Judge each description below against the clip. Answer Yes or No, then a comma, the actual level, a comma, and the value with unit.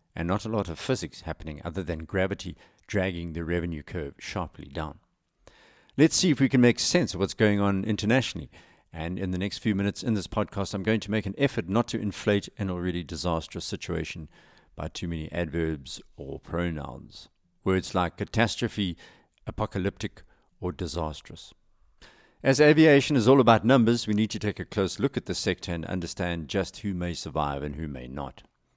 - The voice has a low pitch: Yes, very low, 95 Hz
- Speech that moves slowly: No, average, 185 wpm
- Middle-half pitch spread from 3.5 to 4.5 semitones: Yes, average, 4.2 semitones